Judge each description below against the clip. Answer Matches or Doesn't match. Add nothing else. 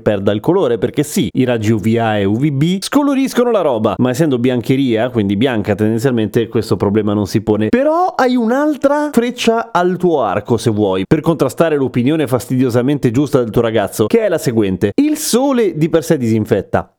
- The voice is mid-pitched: Doesn't match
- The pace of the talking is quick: Matches